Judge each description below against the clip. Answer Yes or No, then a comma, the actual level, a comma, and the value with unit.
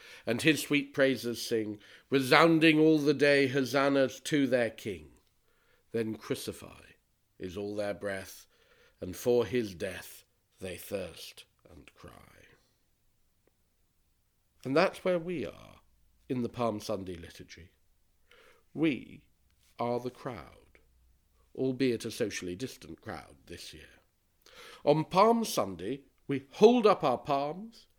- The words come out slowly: Yes, slow, 120 wpm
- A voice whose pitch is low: Yes, low, 115 Hz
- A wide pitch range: Yes, wide, 7.5 semitones